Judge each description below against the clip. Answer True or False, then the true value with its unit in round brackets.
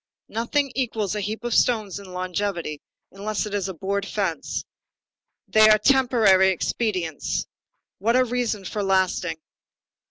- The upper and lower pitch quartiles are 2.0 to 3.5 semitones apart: True (3.2 semitones)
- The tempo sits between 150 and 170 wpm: False (135 wpm)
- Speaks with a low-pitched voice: False (205 Hz)